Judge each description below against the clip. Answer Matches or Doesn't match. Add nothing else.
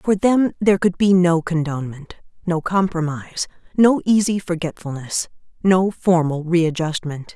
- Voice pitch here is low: Doesn't match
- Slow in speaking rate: Matches